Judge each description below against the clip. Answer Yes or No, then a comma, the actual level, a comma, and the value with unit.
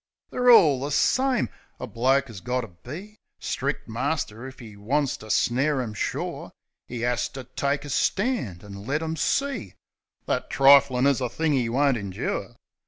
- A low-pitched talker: Yes, low, 130 Hz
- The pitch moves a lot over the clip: No, average, 4.2 semitones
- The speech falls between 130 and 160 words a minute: No, average, 170 wpm